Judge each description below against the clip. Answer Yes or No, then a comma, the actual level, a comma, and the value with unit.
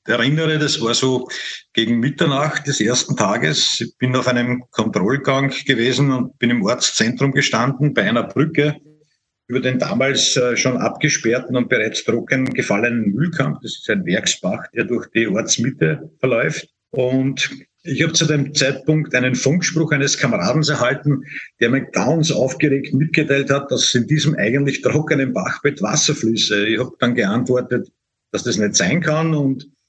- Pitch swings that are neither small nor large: Yes, average, 3.2 semitones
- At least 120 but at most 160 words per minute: Yes, average, 155 wpm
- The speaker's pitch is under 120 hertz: No, low, 135 Hz